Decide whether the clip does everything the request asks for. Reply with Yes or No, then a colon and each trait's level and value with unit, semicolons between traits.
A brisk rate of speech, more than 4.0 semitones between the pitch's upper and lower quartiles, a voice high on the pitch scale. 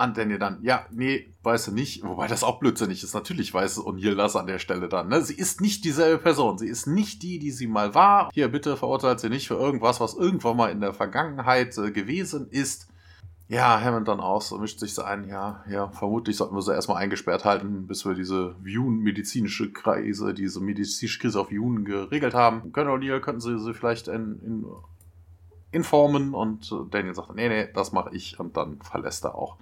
No: fast, 210 wpm; average, 5.1 semitones; low, 115 Hz